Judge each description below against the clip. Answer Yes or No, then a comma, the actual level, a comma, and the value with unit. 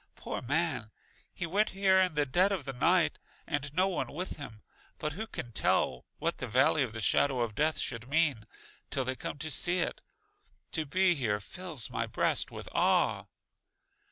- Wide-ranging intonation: Yes, wide, 5.9 semitones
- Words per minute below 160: No, average, 185 wpm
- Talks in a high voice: No, medium, 145 Hz